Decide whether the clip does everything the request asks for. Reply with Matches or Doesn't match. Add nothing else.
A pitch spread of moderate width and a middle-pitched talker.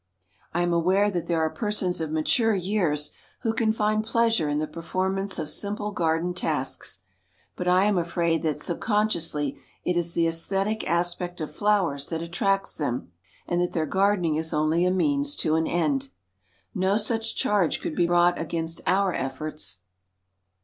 Matches